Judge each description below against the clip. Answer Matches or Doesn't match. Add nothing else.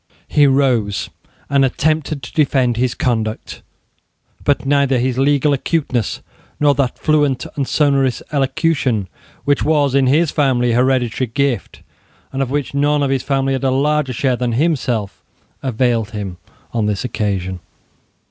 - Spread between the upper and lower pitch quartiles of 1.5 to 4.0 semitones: Matches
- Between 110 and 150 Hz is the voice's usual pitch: Matches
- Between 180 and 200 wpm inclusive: Doesn't match